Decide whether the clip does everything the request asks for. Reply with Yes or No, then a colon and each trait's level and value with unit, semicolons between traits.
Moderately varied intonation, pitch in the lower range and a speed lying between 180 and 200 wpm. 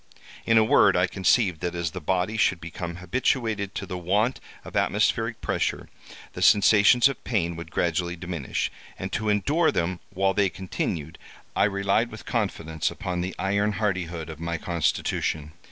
No: average, 3.5 semitones; very low, 95 Hz; average, 160 wpm